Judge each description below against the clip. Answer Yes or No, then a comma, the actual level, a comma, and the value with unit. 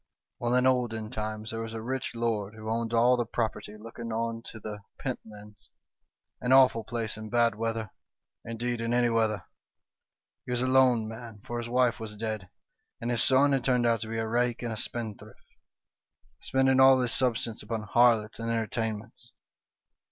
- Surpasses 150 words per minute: Yes, average, 190 wpm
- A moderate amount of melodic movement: No, narrow, 1.9 semitones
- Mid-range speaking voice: No, low, 115 Hz